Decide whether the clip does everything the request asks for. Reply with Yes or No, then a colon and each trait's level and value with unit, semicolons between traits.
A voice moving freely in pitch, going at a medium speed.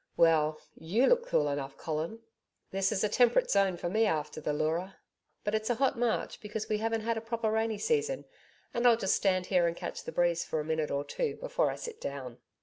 No: wide, 6.2 semitones; fast, 220 wpm